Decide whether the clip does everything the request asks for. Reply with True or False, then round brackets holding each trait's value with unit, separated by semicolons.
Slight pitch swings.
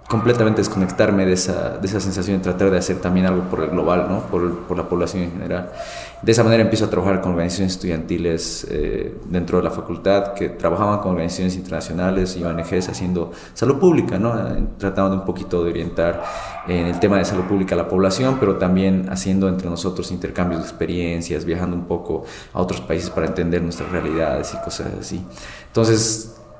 True (2.0 semitones)